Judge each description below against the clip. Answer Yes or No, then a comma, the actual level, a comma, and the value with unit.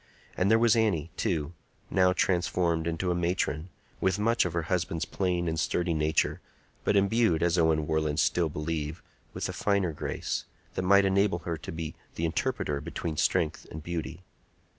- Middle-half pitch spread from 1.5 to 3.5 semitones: Yes, average, 2.9 semitones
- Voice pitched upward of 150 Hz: No, very low, 85 Hz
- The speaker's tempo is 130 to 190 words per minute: Yes, average, 170 wpm